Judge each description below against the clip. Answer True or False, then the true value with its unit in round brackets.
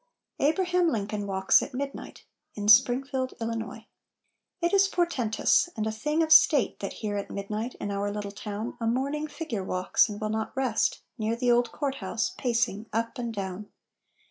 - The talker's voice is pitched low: False (230 Hz)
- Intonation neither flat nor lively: True (4.7 semitones)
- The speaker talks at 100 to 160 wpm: False (170 wpm)